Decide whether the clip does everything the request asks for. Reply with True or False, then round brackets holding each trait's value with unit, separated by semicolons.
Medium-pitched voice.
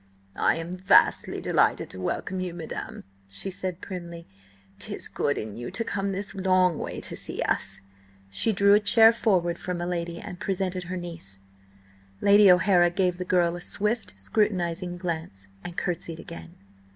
True (180 Hz)